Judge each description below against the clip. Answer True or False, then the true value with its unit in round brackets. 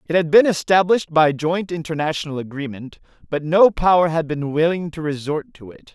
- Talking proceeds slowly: False (180 wpm)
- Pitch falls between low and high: True (160 Hz)